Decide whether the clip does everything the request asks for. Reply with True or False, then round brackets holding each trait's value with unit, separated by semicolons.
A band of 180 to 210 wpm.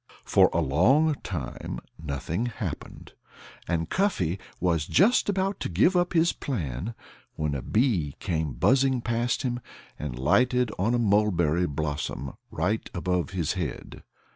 False (140 wpm)